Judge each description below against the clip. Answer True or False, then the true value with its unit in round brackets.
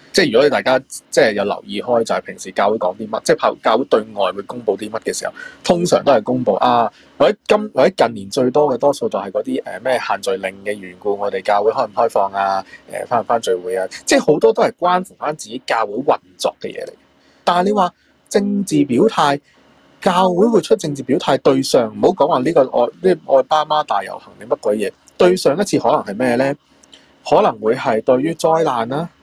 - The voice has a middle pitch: True (180 Hz)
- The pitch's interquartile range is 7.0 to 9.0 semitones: True (8.2 semitones)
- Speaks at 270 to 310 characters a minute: False (325 characters per minute)